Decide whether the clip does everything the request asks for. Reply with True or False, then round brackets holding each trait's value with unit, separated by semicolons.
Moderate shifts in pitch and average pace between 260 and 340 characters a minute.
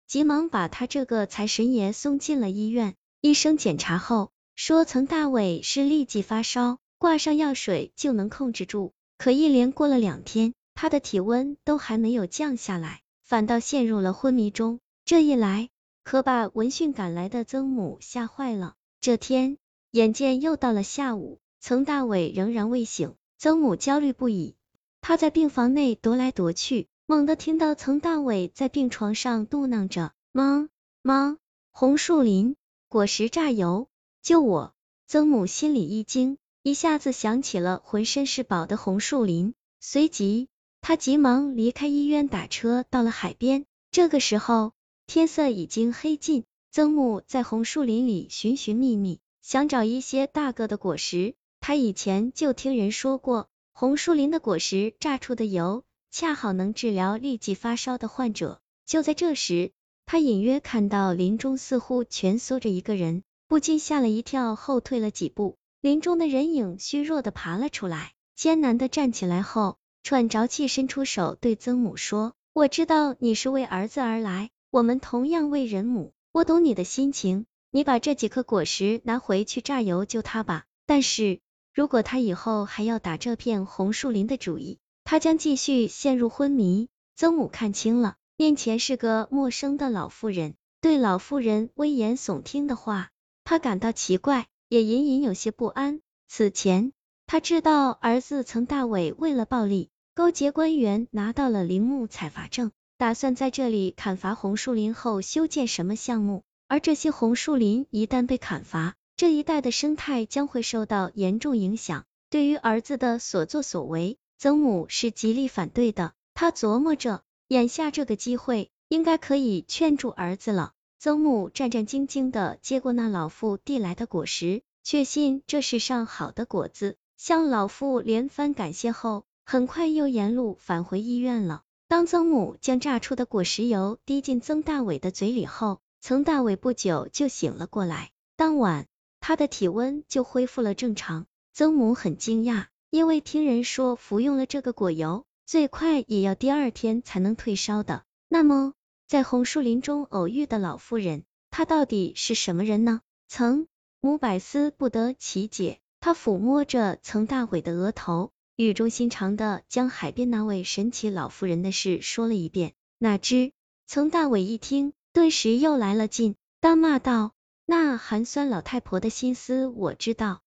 False (5.0 semitones; 245 characters per minute)